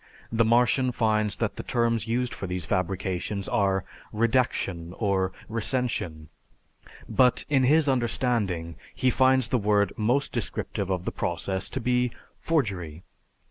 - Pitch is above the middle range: No, low, 110 Hz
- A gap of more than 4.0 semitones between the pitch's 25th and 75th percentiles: Yes, average, 4.7 semitones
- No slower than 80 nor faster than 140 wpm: Yes, slow, 135 wpm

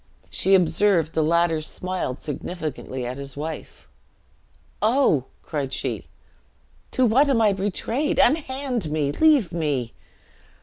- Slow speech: Yes, slow, 120 wpm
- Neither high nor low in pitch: Yes, medium, 170 Hz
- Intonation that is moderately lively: No, wide, 7.2 semitones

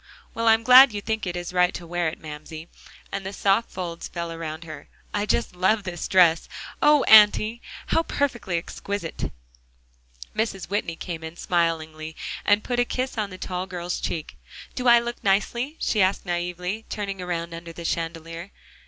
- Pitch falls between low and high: Yes, medium, 180 Hz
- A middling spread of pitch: Yes, average, 4.2 semitones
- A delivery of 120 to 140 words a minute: No, average, 175 wpm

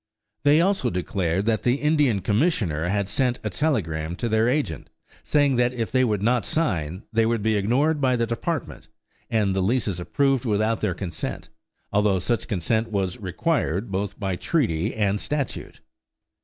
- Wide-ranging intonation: No, average, 4.9 semitones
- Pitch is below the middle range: Yes, low, 110 Hz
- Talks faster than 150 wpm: Yes, average, 165 wpm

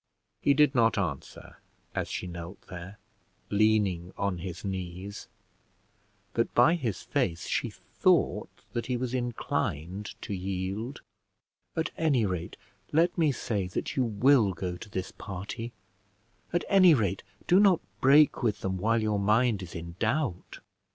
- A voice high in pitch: No, low, 105 Hz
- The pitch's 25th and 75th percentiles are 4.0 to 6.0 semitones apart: Yes, wide, 5.6 semitones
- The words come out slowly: No, average, 145 wpm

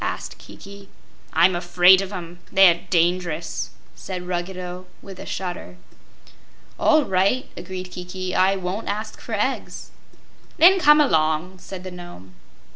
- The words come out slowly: Yes, slow, 130 wpm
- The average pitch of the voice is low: No, medium, 185 Hz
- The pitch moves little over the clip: Yes, narrow, 1.8 semitones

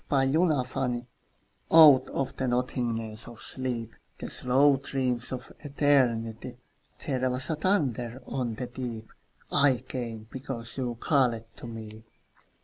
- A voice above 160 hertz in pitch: No, low, 125 Hz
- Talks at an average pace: No, slow, 130 wpm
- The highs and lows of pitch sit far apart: No, narrow, 2.5 semitones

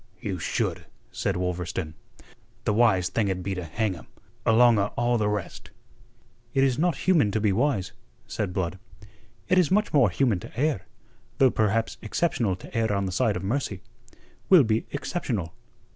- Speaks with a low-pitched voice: Yes, low, 110 Hz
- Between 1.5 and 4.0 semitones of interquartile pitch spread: No, wide, 5.4 semitones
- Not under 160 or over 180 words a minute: Yes, average, 170 wpm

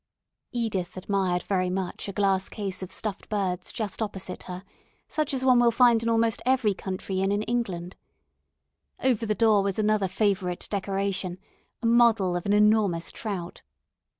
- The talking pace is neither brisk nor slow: Yes, average, 160 wpm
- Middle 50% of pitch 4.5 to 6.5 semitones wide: No, average, 3.2 semitones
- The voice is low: No, high, 200 Hz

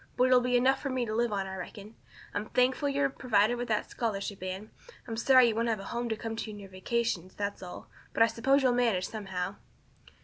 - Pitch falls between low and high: No, high, 225 Hz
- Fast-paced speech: Yes, fast, 240 wpm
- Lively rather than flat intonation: No, average, 3.5 semitones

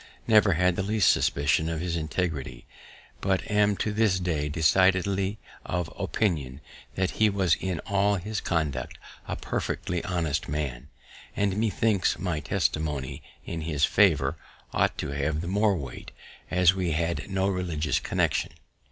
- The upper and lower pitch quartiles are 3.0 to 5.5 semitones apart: Yes, average, 4.1 semitones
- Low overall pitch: Yes, very low, 90 Hz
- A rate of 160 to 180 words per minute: No, average, 145 wpm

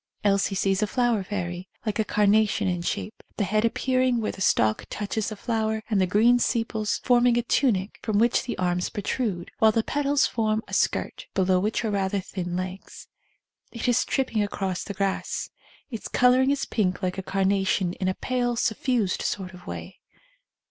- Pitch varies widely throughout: No, average, 3.6 semitones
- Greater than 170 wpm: Yes, average, 185 wpm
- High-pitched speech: Yes, high, 210 Hz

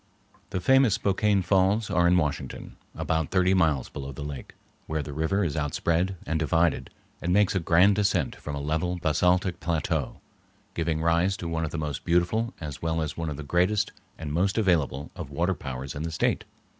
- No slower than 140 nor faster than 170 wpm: No, average, 195 wpm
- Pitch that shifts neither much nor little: Yes, average, 3.4 semitones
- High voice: No, very low, 85 Hz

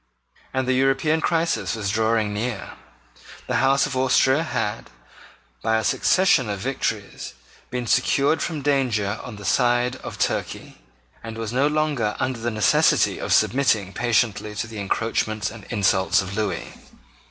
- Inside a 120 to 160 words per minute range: Yes, average, 150 wpm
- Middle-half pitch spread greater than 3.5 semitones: Yes, average, 4.1 semitones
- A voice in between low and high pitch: No, low, 115 Hz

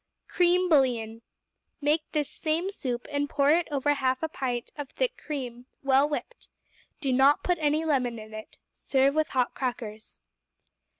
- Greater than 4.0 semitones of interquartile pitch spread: No, average, 3.6 semitones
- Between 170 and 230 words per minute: No, average, 160 wpm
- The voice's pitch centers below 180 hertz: No, very high, 280 Hz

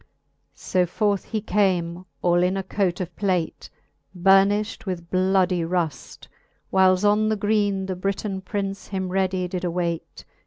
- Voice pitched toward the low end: No, high, 190 Hz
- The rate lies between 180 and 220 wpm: No, average, 150 wpm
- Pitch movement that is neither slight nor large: No, narrow, 1.8 semitones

